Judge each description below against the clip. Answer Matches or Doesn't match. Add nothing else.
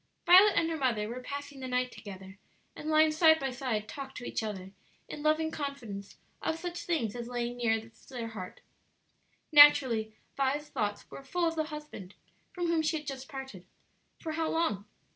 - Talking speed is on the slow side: Doesn't match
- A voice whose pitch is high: Matches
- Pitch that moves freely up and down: Matches